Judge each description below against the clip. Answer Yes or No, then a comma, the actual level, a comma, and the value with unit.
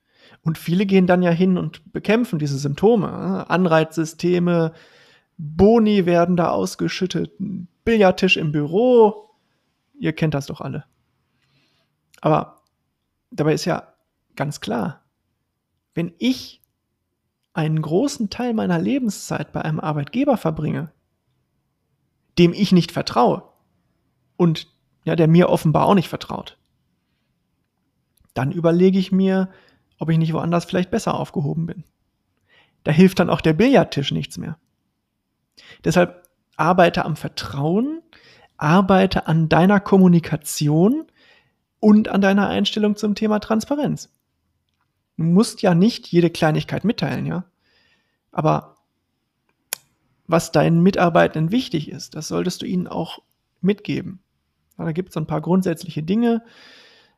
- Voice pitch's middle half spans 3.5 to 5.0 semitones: Yes, average, 3.9 semitones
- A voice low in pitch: No, medium, 175 Hz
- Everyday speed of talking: No, slow, 120 wpm